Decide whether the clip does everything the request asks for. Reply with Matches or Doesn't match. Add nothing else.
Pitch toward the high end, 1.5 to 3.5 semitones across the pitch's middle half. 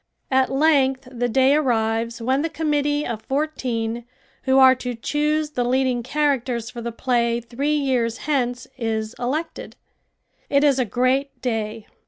Matches